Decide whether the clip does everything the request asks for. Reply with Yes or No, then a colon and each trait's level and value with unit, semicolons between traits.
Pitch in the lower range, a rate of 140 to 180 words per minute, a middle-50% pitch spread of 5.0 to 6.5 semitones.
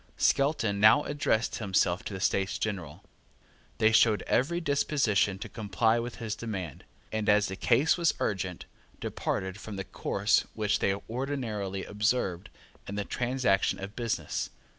No: low, 105 Hz; average, 145 wpm; average, 3.6 semitones